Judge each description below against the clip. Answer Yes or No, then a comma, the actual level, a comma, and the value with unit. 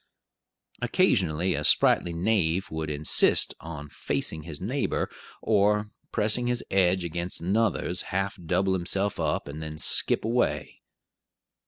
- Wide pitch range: No, average, 4.4 semitones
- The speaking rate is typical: No, slow, 125 wpm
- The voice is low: Yes, very low, 90 Hz